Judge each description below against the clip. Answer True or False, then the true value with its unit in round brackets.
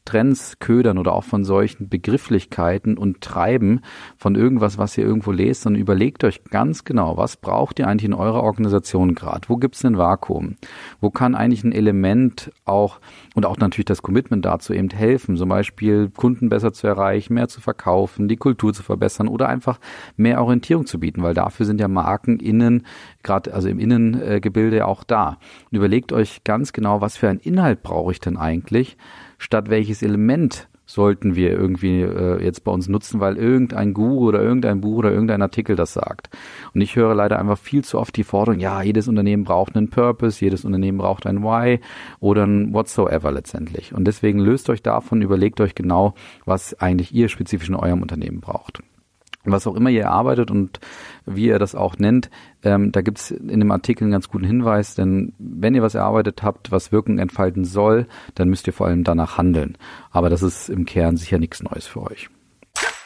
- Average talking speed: False (195 wpm)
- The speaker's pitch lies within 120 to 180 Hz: False (105 Hz)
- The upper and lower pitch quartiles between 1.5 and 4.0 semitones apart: True (3.0 semitones)